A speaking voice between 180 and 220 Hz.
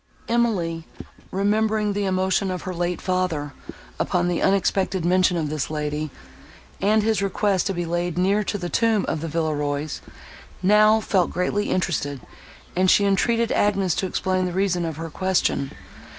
Yes: medium, 185 Hz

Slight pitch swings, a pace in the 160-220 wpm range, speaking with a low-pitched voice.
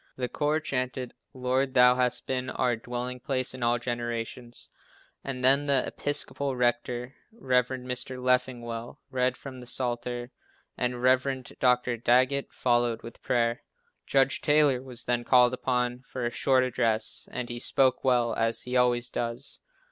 No: narrow, 1.3 semitones; average, 150 wpm; low, 125 Hz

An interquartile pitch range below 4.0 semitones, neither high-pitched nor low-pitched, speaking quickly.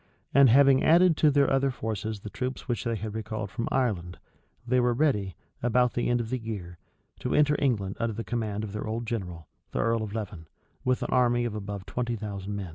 No: average, 3.5 semitones; low, 115 Hz; fast, 215 wpm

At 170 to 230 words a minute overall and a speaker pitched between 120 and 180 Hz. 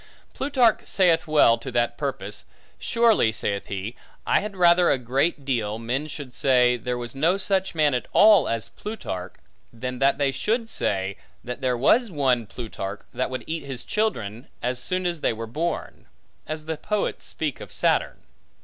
Yes: average, 175 wpm; low, 135 Hz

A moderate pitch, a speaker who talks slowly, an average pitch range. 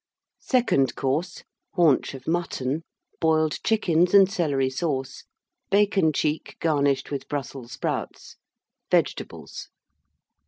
Yes: medium, 155 Hz; slow, 95 wpm; average, 4.5 semitones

